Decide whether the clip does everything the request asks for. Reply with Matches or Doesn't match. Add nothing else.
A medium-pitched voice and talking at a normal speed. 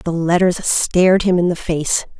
Matches